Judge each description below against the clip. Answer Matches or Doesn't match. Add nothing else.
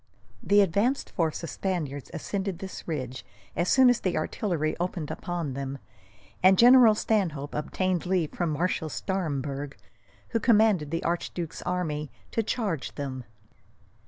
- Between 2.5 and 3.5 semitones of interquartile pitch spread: Doesn't match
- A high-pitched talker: Doesn't match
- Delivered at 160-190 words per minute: Doesn't match